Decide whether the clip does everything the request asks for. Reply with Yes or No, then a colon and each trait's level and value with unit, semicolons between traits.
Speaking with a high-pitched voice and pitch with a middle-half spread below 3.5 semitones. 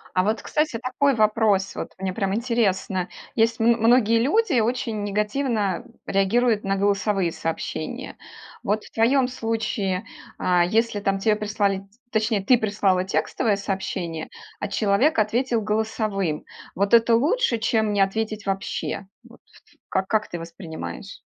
Yes: high, 210 Hz; average, 2.8 semitones